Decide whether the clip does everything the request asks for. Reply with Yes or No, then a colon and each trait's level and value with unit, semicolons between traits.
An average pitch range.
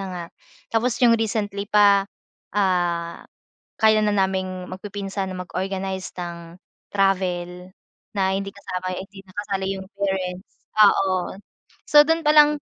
No: narrow, 1.8 semitones